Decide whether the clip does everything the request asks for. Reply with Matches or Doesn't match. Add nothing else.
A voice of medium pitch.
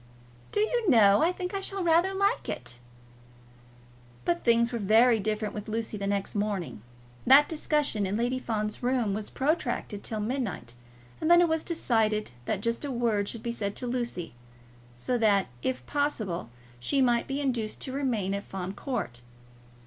Doesn't match